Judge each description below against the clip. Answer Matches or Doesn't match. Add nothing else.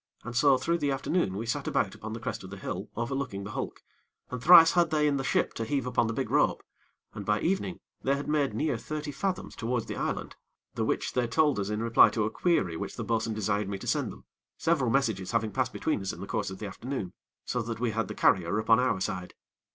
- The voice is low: Matches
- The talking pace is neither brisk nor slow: Doesn't match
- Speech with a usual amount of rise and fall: Matches